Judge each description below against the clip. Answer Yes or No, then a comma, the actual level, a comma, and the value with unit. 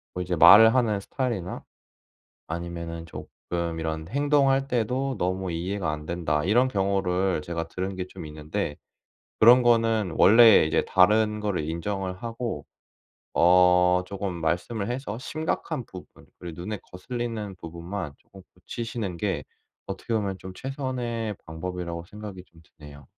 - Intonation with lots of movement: No, average, 4.8 semitones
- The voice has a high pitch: No, very low, 95 Hz